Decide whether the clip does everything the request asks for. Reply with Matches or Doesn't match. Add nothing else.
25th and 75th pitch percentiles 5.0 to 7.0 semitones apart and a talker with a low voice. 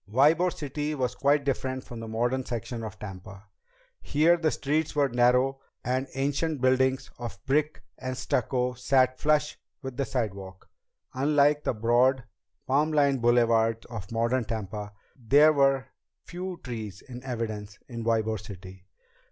Doesn't match